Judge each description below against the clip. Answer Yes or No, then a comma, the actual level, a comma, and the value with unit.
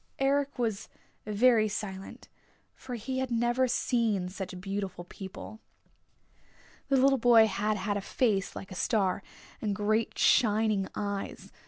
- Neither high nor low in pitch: No, high, 215 Hz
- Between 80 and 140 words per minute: Yes, slow, 135 wpm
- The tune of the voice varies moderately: Yes, average, 3.6 semitones